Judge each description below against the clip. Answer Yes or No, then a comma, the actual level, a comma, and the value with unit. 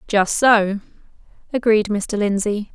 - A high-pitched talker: Yes, high, 210 Hz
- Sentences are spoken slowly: Yes, slow, 110 wpm